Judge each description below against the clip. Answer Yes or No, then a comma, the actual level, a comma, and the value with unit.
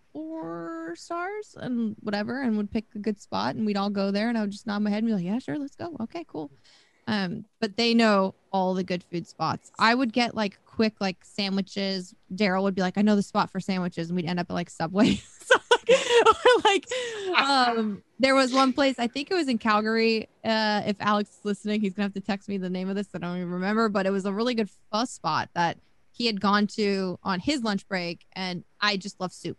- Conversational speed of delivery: No, fast, 245 wpm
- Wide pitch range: No, average, 3.4 semitones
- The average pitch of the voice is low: No, high, 210 Hz